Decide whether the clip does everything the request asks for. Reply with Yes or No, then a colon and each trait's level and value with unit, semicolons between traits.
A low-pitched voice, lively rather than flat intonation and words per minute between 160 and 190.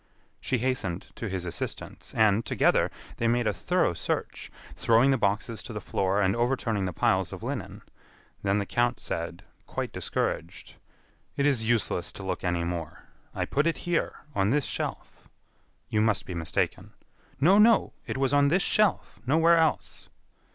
Yes: low, 115 Hz; wide, 6.2 semitones; average, 165 wpm